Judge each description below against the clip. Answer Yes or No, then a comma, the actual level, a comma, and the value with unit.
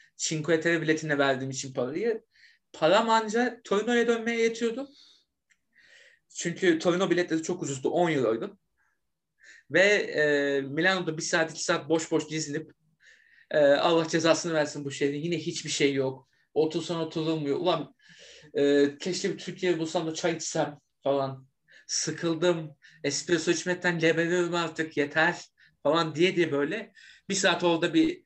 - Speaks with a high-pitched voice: No, medium, 165 Hz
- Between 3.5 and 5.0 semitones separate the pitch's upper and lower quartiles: No, average, 2.9 semitones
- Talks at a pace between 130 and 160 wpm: Yes, fast, 140 wpm